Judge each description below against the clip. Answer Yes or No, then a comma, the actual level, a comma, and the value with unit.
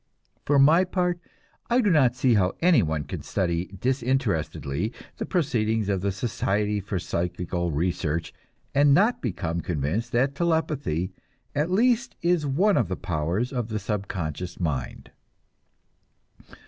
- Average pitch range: No, wide, 8.5 semitones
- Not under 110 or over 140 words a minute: Yes, slow, 135 wpm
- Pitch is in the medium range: No, low, 110 Hz